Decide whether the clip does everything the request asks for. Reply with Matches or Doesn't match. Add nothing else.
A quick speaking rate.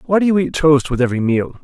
Matches